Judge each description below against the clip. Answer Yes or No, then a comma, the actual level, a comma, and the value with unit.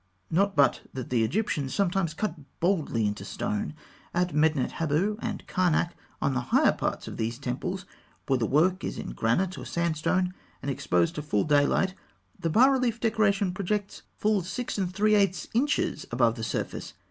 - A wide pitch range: Yes, wide, 6.4 semitones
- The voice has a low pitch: No, medium, 175 Hz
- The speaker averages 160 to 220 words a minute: Yes, average, 170 wpm